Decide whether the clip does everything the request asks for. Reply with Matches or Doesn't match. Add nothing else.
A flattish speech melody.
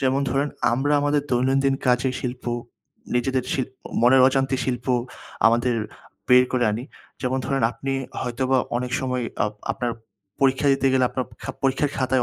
Matches